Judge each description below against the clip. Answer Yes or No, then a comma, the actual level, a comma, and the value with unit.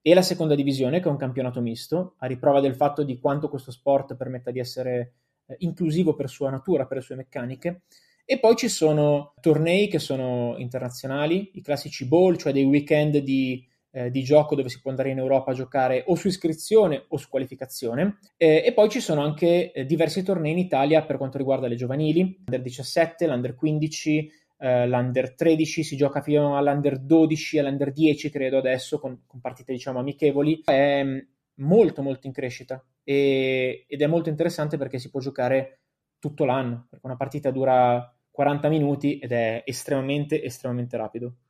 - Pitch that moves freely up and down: No, average, 3.2 semitones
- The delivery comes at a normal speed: No, fast, 180 wpm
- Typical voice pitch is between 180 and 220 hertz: No, medium, 140 Hz